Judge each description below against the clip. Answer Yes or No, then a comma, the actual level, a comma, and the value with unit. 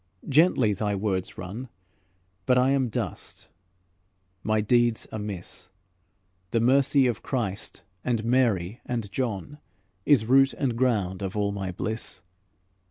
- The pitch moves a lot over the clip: No, average, 4.2 semitones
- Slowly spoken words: Yes, slow, 125 wpm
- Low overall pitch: Yes, low, 110 Hz